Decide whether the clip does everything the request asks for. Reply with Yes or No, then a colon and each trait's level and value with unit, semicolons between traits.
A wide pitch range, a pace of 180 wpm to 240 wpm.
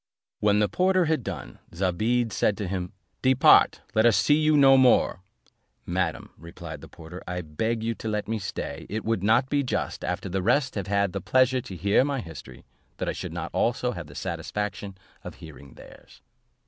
Yes: wide, 5.7 semitones; average, 200 wpm